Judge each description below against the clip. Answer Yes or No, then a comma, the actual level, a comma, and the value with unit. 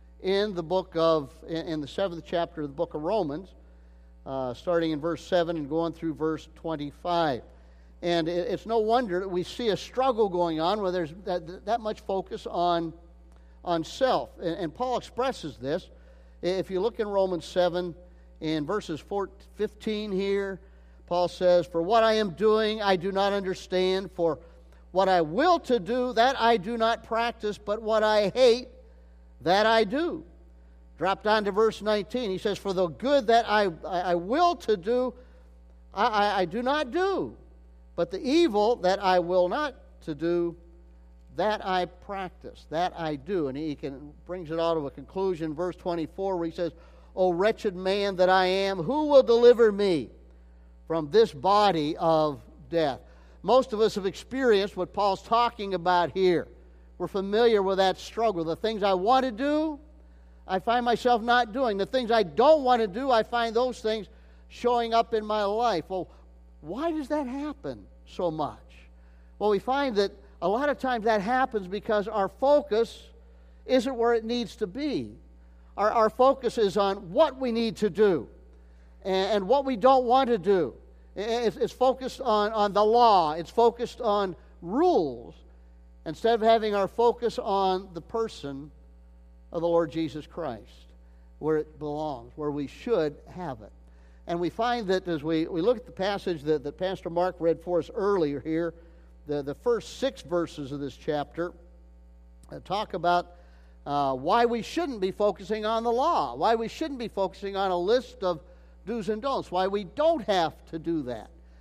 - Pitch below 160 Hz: No, medium, 185 Hz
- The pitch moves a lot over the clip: Yes, wide, 6.5 semitones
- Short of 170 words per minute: No, average, 180 wpm